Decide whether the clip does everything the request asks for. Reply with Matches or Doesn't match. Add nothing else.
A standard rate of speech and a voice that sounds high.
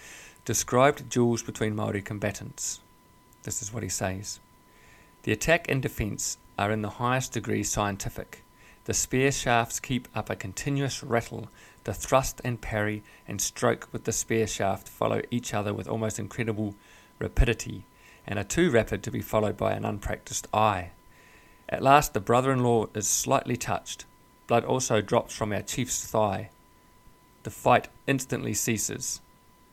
Doesn't match